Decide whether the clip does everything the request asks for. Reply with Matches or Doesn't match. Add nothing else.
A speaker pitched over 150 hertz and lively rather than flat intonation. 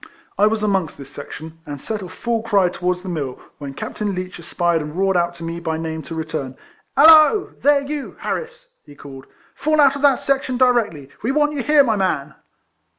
Matches